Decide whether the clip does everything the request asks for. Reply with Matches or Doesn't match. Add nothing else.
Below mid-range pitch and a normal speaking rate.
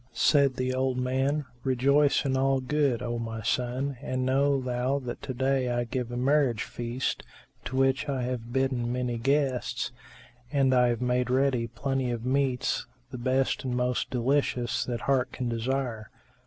Matches